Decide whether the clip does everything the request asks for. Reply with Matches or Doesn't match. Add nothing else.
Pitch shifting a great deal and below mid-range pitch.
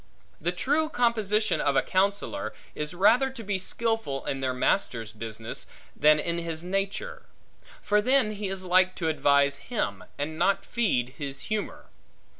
Doesn't match